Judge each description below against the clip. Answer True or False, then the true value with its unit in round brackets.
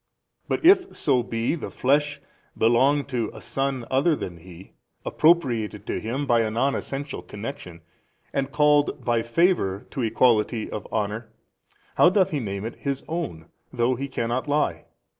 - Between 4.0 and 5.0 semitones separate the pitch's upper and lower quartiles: True (4.5 semitones)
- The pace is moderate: True (160 wpm)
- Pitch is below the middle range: True (130 Hz)